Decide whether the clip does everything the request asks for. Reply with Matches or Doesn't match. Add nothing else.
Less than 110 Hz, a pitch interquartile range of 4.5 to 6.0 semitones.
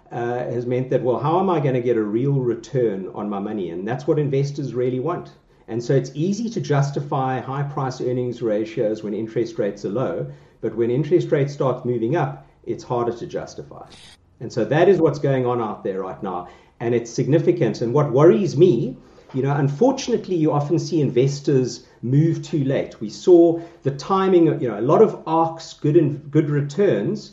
Doesn't match